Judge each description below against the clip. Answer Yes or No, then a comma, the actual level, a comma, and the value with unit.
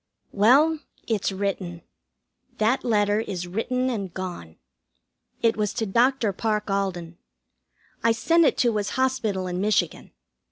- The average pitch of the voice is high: Yes, high, 210 Hz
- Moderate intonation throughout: Yes, average, 3.8 semitones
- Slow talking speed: Yes, slow, 130 wpm